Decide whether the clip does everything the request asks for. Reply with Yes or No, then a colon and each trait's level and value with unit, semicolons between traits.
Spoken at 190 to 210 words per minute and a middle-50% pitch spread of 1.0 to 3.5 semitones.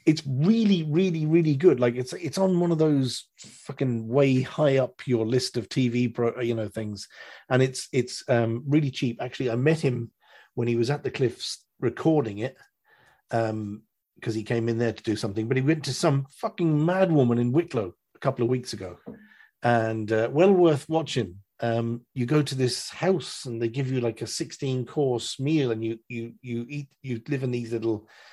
No: fast, 205 wpm; average, 4.0 semitones